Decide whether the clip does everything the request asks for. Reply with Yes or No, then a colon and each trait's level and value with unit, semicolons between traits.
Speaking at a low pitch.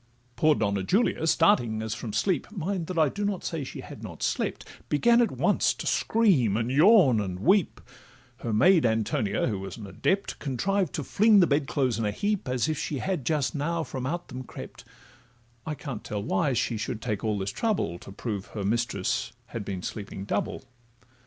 Yes: low, 130 Hz